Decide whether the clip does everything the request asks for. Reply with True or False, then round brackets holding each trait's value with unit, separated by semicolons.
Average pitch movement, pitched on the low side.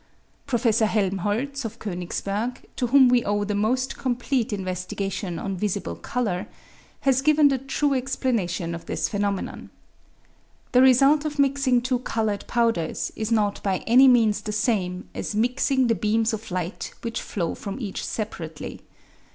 False (4.3 semitones; 225 Hz)